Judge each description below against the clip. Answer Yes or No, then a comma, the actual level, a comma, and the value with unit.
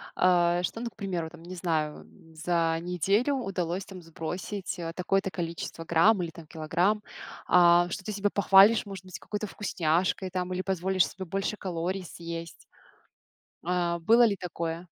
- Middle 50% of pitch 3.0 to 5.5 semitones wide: No, narrow, 2.6 semitones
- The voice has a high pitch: No, medium, 180 Hz